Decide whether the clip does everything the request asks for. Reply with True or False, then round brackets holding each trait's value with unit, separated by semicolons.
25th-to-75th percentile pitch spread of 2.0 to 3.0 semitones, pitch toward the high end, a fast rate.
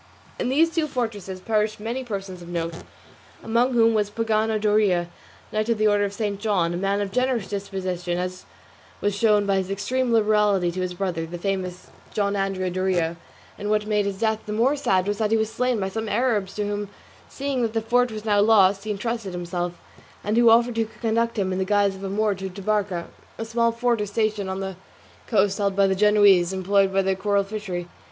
True (2.6 semitones; 205 Hz; 215 wpm)